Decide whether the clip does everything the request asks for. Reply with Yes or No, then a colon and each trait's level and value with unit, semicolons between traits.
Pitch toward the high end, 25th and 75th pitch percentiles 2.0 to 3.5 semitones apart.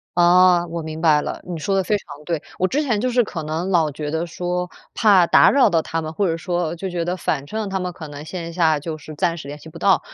No: medium, 175 Hz; average, 2.8 semitones